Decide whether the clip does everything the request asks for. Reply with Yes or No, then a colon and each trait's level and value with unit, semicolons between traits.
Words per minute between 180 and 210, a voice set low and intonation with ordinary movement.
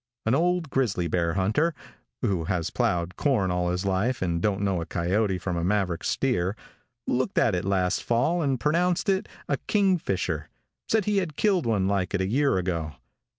No: average, 185 wpm; low, 100 Hz; wide, 7.8 semitones